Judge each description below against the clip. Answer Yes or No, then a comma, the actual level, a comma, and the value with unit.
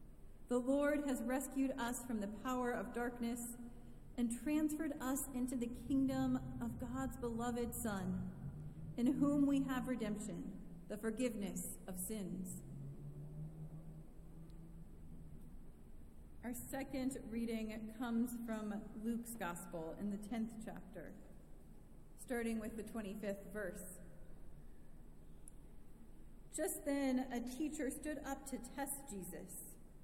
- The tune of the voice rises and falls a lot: Yes, wide, 7.6 semitones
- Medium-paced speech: No, slow, 110 wpm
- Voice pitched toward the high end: Yes, high, 220 Hz